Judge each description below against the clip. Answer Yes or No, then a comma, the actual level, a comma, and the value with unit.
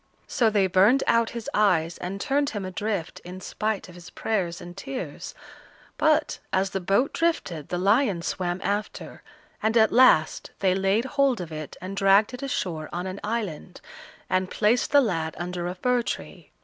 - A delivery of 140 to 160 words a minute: No, average, 175 wpm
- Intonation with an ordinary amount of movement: Yes, average, 4.6 semitones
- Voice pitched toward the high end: Yes, high, 195 Hz